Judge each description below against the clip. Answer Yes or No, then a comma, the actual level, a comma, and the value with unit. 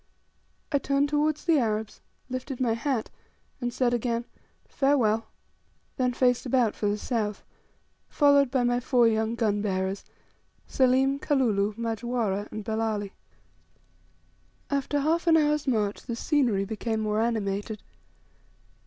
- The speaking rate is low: Yes, slow, 125 wpm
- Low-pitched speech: No, high, 235 Hz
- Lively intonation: No, average, 3.9 semitones